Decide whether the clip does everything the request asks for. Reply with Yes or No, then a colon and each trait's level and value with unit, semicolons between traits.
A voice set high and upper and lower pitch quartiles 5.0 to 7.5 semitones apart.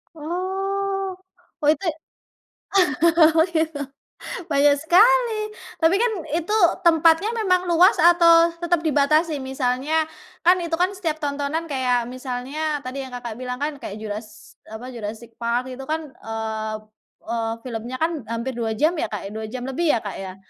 Yes: very high, 295 Hz; wide, 5.5 semitones